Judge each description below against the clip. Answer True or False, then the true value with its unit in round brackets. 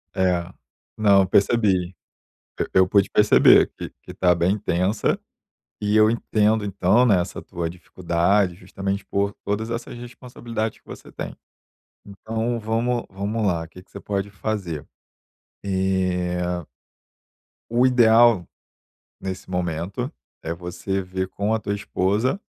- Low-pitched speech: True (100 Hz)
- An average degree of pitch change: True (3.2 semitones)